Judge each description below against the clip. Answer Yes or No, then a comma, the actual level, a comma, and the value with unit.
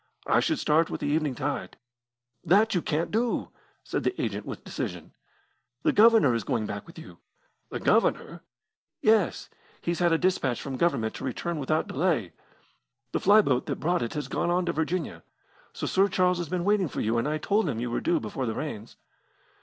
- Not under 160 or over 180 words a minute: No, average, 200 wpm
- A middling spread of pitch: No, wide, 6.0 semitones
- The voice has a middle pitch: Yes, medium, 165 Hz